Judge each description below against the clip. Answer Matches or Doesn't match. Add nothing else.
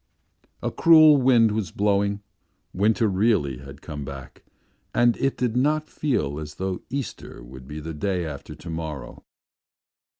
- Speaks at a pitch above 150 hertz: Doesn't match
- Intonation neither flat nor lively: Doesn't match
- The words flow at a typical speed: Matches